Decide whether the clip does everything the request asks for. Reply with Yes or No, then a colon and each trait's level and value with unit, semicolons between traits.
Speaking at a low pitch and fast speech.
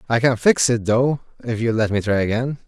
Yes: low, 120 Hz; fast, 245 wpm